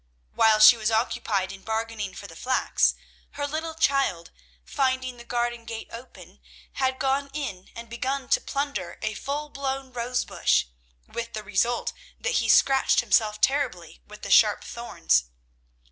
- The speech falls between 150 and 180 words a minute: Yes, average, 155 wpm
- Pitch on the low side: No, high, 240 Hz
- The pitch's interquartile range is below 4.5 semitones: Yes, average, 3.9 semitones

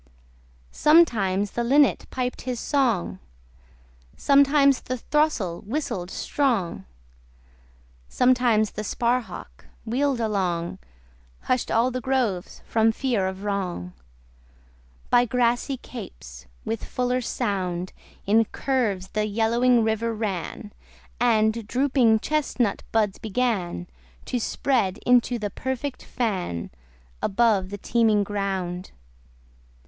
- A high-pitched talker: Yes, high, 225 Hz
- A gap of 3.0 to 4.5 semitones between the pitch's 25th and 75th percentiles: Yes, average, 4.2 semitones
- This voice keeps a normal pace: No, slow, 100 wpm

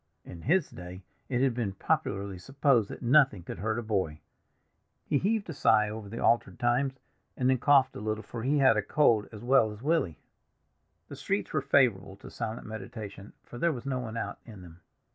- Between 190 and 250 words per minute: Yes, average, 200 wpm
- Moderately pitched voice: No, low, 115 Hz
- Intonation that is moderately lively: Yes, average, 4.7 semitones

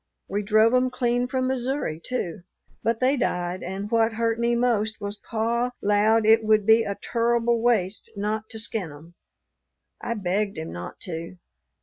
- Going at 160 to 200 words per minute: Yes, average, 165 wpm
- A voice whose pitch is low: No, high, 220 Hz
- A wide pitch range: No, average, 2.9 semitones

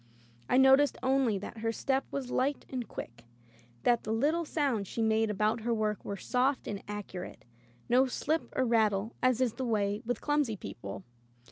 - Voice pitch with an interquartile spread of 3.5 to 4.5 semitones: Yes, average, 3.9 semitones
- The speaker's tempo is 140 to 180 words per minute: Yes, average, 175 wpm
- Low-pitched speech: No, high, 230 Hz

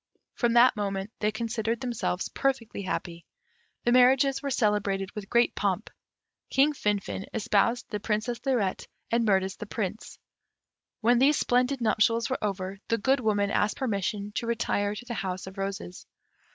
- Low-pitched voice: No, high, 220 Hz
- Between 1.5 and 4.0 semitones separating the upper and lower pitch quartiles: Yes, average, 3.4 semitones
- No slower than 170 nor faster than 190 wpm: No, average, 155 wpm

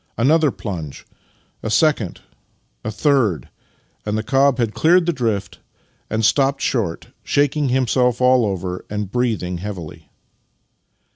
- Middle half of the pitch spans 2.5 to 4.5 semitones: No, average, 4.9 semitones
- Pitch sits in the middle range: No, low, 115 Hz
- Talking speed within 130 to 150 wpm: Yes, average, 145 wpm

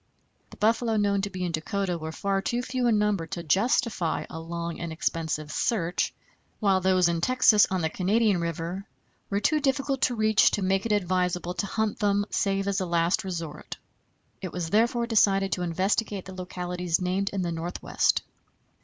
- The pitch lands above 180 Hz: Yes, high, 190 Hz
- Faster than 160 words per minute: Yes, average, 180 wpm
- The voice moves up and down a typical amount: Yes, average, 3.4 semitones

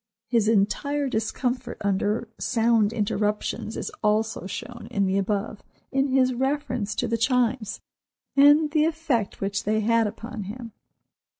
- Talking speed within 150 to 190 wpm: No, slow, 135 wpm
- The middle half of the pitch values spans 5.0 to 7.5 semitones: No, average, 3.6 semitones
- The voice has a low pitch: No, high, 230 Hz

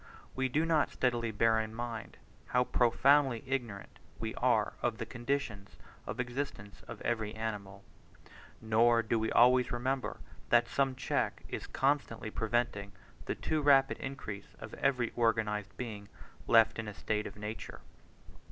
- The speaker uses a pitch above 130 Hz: No, low, 115 Hz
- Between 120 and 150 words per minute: Yes, average, 145 wpm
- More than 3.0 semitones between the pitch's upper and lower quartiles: No, average, 2.7 semitones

